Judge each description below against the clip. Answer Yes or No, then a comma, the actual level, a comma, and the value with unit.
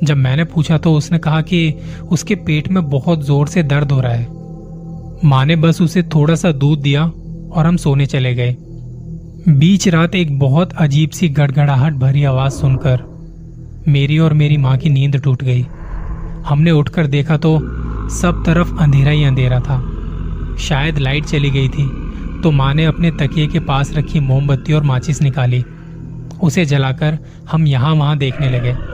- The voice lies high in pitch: No, medium, 150 Hz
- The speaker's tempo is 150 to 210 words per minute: Yes, average, 170 wpm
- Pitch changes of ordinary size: Yes, average, 3.0 semitones